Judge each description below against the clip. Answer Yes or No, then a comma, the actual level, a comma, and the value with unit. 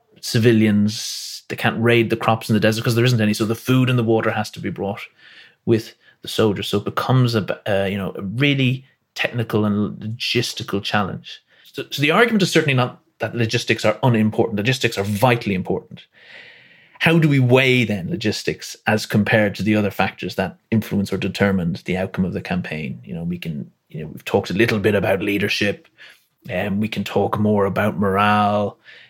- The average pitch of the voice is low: Yes, low, 110 Hz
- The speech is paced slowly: No, average, 200 wpm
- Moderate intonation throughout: Yes, average, 3.2 semitones